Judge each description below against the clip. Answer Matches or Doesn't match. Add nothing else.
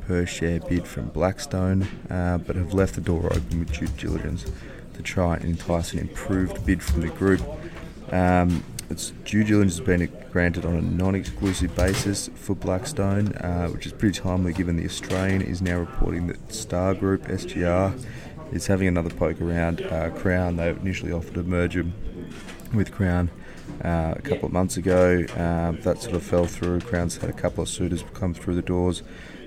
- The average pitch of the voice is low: Matches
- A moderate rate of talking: Matches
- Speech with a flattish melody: Matches